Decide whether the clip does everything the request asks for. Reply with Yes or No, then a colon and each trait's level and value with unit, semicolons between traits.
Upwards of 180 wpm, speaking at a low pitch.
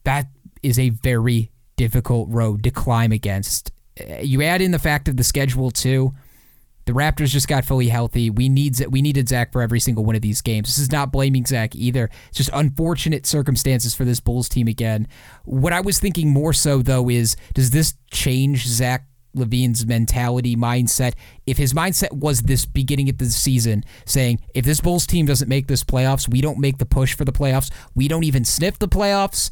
Yes: average, 200 wpm; low, 130 Hz